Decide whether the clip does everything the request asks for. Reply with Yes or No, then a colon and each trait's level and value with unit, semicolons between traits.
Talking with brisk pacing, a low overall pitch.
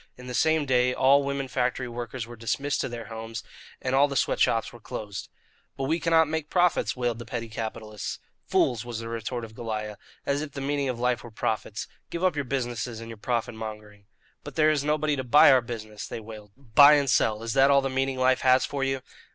Yes: fast, 225 wpm; low, 125 Hz